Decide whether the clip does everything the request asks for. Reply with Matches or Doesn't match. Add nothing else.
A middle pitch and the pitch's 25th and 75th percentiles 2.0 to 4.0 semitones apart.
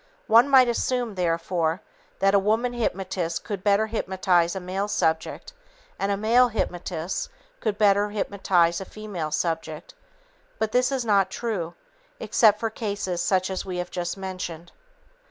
Doesn't match